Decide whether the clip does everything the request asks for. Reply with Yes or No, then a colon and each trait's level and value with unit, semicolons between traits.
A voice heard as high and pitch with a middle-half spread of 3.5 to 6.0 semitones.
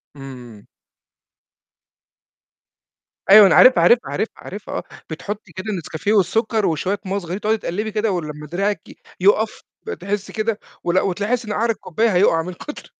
Yes: high, 200 Hz; average, 3.8 semitones